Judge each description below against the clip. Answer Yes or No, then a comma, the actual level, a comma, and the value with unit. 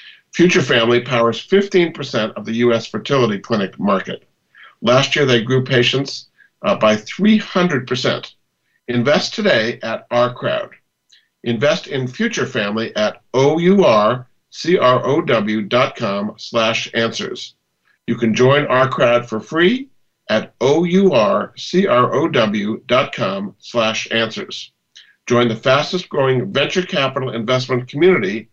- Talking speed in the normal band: No, slow, 105 wpm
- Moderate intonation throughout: No, wide, 6.7 semitones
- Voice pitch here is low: Yes, low, 130 Hz